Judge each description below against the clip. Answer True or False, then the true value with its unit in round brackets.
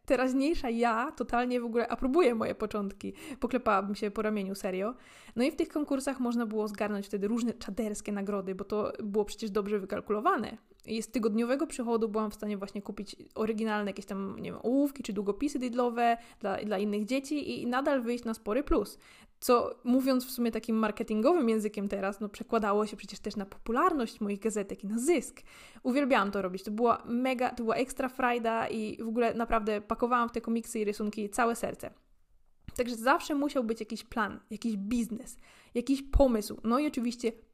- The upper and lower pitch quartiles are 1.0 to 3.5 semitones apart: True (2.9 semitones)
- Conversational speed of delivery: False (180 wpm)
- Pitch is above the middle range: True (230 Hz)